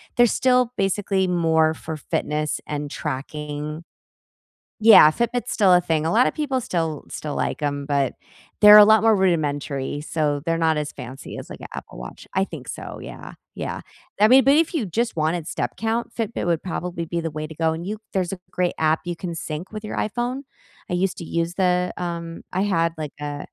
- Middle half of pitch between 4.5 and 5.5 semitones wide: Yes, average, 5.2 semitones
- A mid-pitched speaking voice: Yes, medium, 170 Hz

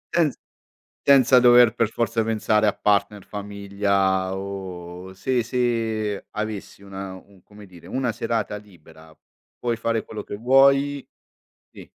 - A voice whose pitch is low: Yes, low, 105 Hz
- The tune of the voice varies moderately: Yes, average, 3.2 semitones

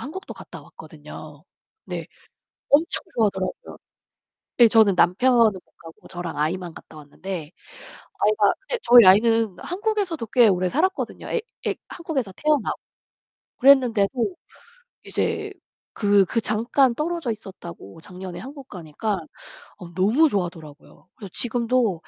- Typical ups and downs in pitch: No, wide, 6.4 semitones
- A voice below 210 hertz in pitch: No, high, 215 Hz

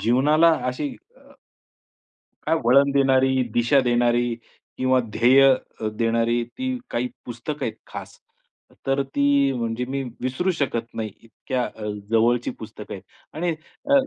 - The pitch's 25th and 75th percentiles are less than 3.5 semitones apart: Yes, average, 2.8 semitones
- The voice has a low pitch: Yes, low, 130 Hz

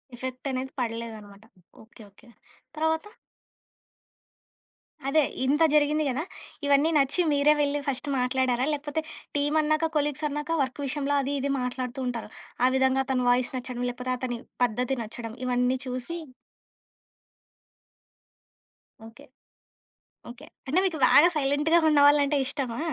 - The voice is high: Yes, very high, 270 Hz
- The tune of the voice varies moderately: Yes, average, 3.0 semitones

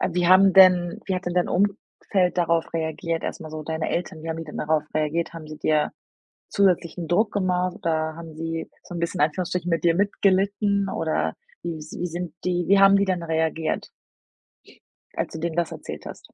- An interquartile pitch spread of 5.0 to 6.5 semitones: No, narrow, 2.4 semitones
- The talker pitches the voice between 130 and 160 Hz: No, medium, 170 Hz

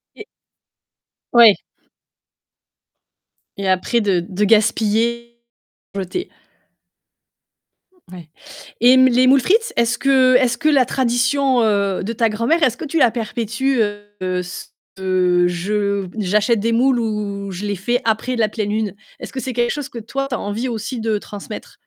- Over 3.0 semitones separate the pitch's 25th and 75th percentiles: Yes, average, 3.7 semitones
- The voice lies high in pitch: Yes, high, 225 Hz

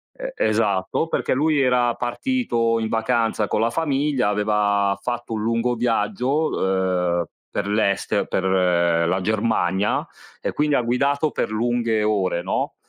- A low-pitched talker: Yes, low, 110 Hz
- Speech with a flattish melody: No, average, 4.0 semitones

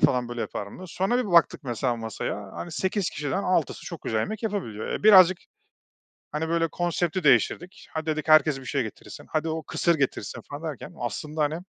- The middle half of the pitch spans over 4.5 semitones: Yes, wide, 5.5 semitones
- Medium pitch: Yes, medium, 155 Hz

